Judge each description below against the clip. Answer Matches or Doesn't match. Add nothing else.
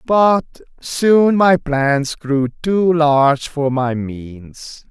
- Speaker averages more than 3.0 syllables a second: Doesn't match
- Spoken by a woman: Doesn't match